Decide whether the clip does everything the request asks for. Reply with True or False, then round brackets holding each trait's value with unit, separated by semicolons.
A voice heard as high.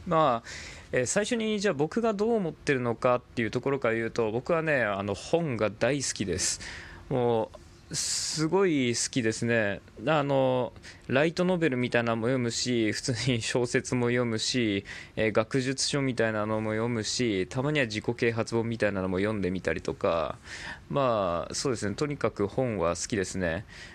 False (120 Hz)